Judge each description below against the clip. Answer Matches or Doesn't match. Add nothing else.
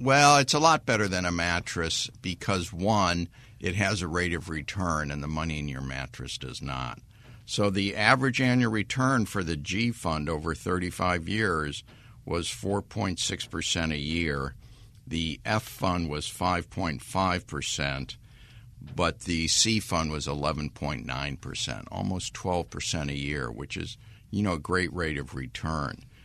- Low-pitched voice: Matches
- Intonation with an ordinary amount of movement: Doesn't match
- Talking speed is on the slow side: Doesn't match